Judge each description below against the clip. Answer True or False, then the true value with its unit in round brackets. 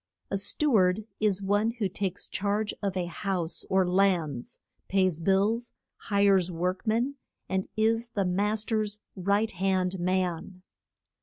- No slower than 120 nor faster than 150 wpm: True (140 wpm)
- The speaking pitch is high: True (195 Hz)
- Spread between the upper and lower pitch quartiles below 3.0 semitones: True (2.4 semitones)